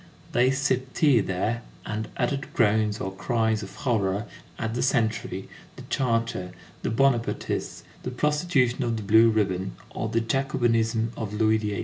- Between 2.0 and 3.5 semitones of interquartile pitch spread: Yes, average, 2.8 semitones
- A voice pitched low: Yes, low, 115 Hz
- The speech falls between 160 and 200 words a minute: No, average, 150 wpm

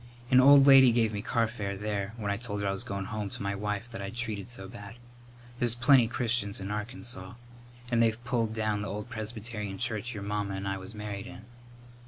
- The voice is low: Yes, low, 105 Hz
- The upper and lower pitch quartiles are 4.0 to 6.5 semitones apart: No, average, 2.9 semitones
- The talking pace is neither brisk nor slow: No, fast, 215 wpm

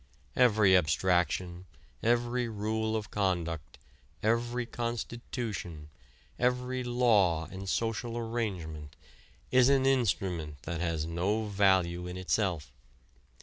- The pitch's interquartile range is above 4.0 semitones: Yes, average, 5.3 semitones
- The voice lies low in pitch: Yes, low, 105 Hz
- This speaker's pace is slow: Yes, slow, 100 wpm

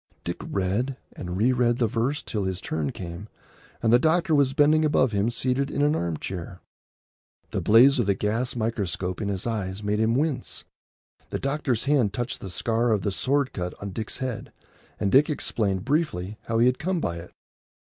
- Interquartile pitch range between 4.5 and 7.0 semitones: Yes, wide, 5.5 semitones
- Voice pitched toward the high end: No, low, 115 Hz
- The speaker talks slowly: No, average, 195 wpm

